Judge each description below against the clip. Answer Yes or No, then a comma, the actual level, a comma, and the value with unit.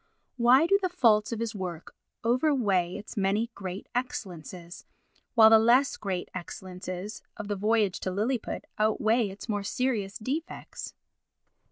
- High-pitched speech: Yes, high, 215 Hz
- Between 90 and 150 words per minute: Yes, average, 140 wpm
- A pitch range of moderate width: Yes, average, 4.0 semitones